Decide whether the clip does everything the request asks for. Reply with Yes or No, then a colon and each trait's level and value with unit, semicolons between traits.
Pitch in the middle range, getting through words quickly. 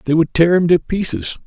Yes: medium, 160 Hz; fast, 245 wpm